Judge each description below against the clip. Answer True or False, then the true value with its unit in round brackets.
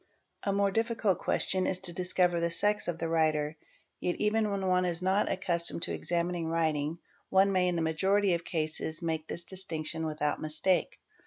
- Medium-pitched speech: True (175 Hz)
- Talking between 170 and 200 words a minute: True (185 wpm)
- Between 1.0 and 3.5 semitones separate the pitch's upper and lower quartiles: True (2.9 semitones)